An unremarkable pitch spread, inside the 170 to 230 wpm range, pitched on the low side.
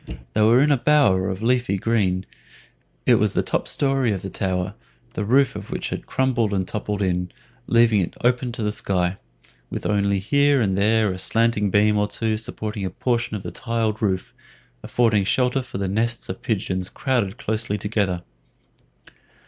Yes: average, 3.5 semitones; average, 180 wpm; low, 105 Hz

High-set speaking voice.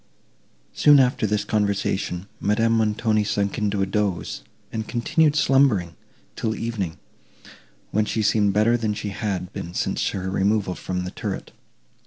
No: low, 105 Hz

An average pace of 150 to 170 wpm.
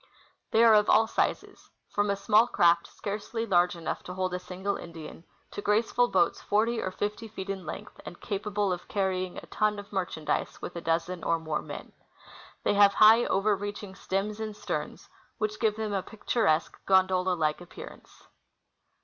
No: average, 180 wpm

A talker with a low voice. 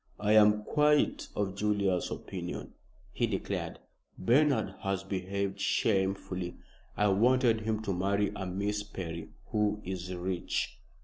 Yes: low, 100 Hz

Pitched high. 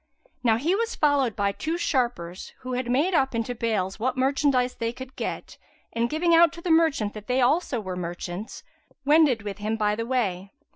Yes: high, 245 Hz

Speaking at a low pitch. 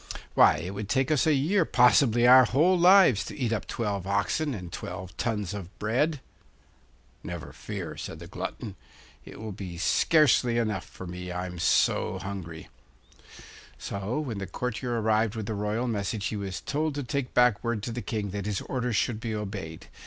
Yes: low, 110 Hz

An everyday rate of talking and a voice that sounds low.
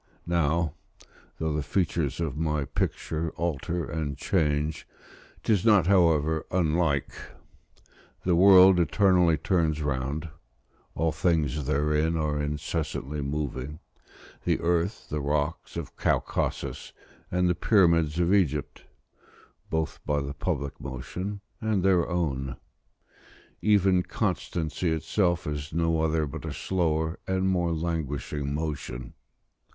No: slow, 115 wpm; very low, 80 Hz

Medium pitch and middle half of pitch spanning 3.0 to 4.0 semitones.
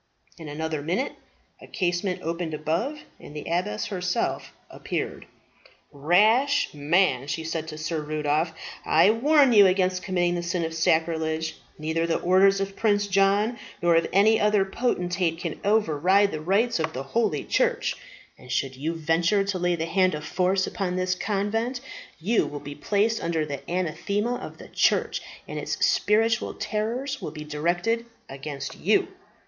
No: medium, 180 Hz; average, 4.5 semitones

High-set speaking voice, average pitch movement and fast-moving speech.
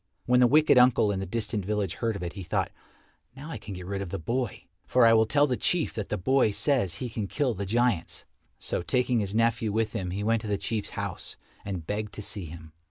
No: low, 110 Hz; average, 3.9 semitones; fast, 245 wpm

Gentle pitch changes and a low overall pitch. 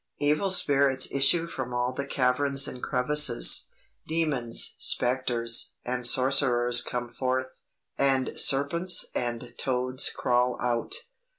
Yes: narrow, 2.2 semitones; low, 130 Hz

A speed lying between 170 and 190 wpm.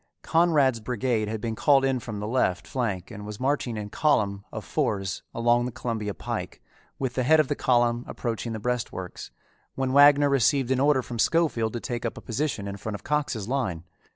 No: average, 200 wpm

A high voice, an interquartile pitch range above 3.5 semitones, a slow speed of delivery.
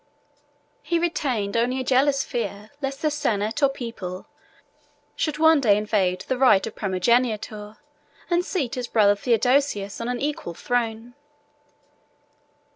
Yes: high, 240 Hz; average, 4.6 semitones; slow, 130 wpm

